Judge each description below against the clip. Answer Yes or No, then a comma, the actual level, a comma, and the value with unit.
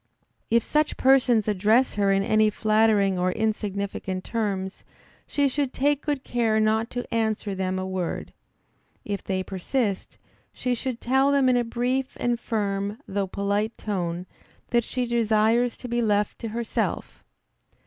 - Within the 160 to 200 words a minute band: No, average, 150 wpm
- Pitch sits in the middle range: No, high, 220 Hz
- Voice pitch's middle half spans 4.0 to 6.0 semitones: No, average, 3.4 semitones